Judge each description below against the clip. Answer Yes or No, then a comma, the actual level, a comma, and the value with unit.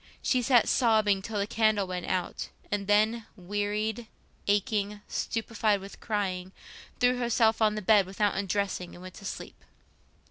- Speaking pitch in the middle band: No, high, 205 Hz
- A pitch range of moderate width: No, narrow, 2.1 semitones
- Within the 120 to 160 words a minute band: Yes, average, 150 wpm